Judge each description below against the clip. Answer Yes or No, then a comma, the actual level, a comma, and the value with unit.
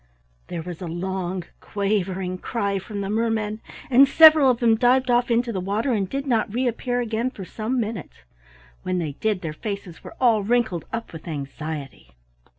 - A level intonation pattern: No, average, 4.7 semitones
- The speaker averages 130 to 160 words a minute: No, average, 175 wpm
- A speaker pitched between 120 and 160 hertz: No, high, 215 Hz